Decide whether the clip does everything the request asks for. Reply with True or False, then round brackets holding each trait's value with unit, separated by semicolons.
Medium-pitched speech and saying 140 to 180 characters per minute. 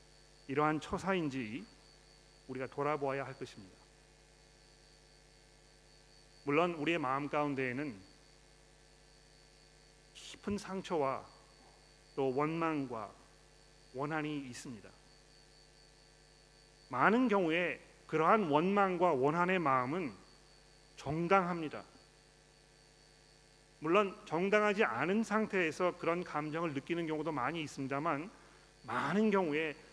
False (155 Hz; 210 characters per minute)